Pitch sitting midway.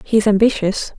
No: high, 210 Hz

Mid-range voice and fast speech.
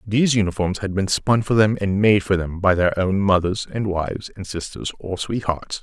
No: low, 100 Hz; fast, 215 wpm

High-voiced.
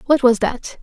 Yes: very high, 250 Hz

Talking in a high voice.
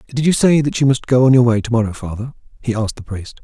No: low, 120 Hz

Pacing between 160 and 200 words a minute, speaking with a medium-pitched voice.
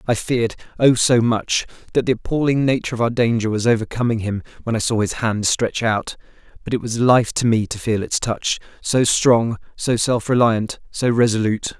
No: average, 195 wpm; low, 115 Hz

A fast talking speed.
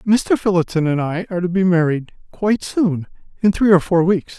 No: average, 190 wpm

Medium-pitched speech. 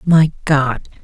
Yes: medium, 150 Hz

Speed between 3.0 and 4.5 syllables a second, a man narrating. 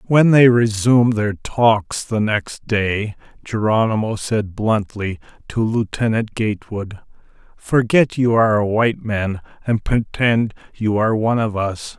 Yes: 4.2 syllables/s; male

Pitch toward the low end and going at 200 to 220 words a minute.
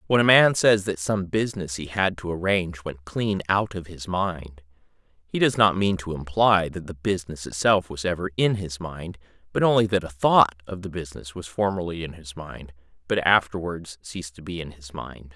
Yes: very low, 90 Hz; fast, 205 wpm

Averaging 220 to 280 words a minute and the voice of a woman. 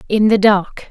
No: average, 200 wpm; female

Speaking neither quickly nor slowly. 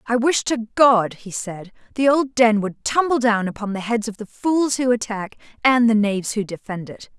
No: fast, 215 wpm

